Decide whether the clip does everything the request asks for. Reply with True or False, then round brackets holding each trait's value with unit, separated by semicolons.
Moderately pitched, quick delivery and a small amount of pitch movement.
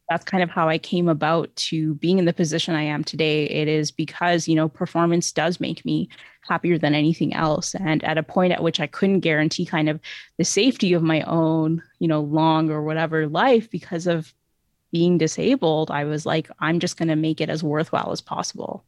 True (160 Hz; 215 wpm; 1.7 semitones)